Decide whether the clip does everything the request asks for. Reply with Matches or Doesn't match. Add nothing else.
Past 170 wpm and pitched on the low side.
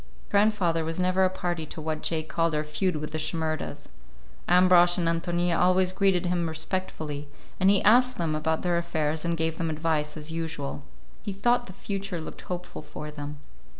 Doesn't match